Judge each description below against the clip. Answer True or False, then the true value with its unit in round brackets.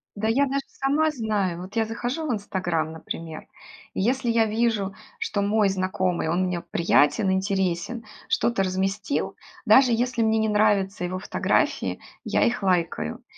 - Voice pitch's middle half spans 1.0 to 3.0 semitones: False (3.7 semitones)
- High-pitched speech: True (205 Hz)